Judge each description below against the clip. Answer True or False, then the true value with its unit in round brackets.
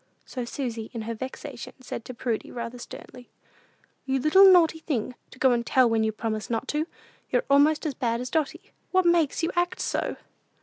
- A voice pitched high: True (260 Hz)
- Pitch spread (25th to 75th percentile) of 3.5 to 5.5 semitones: True (5.2 semitones)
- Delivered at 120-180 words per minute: False (190 wpm)